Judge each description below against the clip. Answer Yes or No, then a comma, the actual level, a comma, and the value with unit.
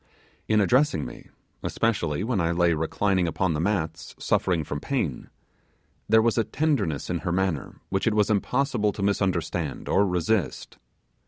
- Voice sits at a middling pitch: No, very low, 95 Hz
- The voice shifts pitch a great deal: No, average, 4.7 semitones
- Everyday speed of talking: Yes, average, 155 wpm